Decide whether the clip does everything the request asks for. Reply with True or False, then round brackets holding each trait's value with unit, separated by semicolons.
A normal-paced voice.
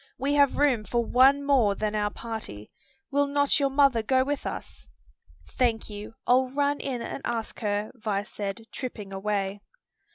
True (165 wpm)